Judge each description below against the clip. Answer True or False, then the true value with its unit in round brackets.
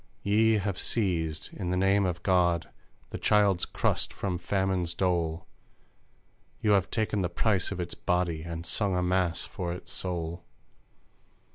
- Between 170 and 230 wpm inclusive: False (150 wpm)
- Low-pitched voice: True (90 Hz)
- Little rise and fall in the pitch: True (2.3 semitones)